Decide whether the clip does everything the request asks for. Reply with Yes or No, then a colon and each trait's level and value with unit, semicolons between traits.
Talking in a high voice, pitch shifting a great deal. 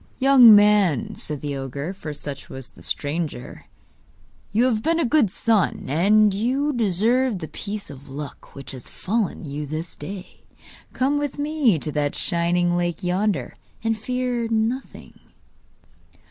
Yes: high, 200 Hz; wide, 7.5 semitones